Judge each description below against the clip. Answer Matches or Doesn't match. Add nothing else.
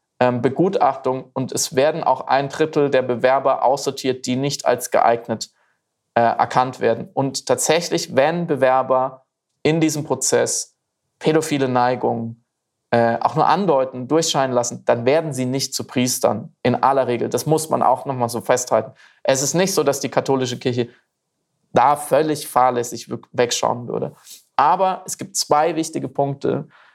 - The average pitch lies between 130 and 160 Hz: Matches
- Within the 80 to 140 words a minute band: Doesn't match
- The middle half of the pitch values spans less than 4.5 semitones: Matches